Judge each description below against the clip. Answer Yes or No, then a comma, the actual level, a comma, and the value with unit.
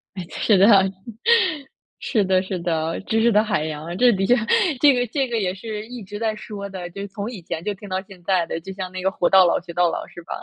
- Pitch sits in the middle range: No, high, 195 Hz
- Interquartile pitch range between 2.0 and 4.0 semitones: Yes, average, 3.2 semitones